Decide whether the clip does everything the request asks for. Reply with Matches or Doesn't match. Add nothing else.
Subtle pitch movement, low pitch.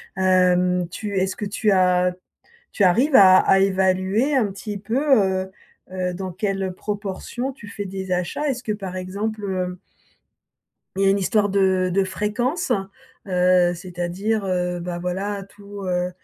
Doesn't match